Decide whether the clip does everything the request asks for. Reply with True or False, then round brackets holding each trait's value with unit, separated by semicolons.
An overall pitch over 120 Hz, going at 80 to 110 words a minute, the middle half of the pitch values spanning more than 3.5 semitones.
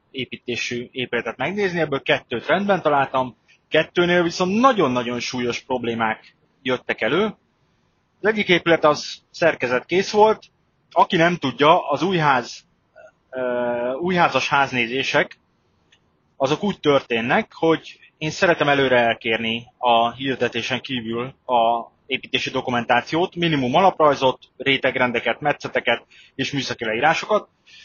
True (130 Hz; 105 wpm; 5.0 semitones)